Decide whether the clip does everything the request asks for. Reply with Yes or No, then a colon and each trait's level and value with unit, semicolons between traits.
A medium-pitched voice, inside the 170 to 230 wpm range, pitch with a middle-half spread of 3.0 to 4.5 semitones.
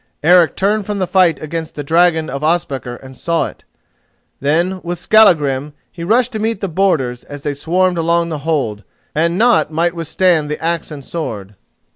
Yes: medium, 165 Hz; average, 185 wpm; average, 3.7 semitones